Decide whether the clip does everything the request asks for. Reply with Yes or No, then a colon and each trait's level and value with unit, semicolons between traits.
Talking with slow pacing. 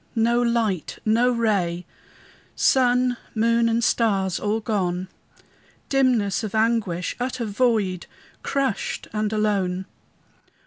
Yes: slow, 100 wpm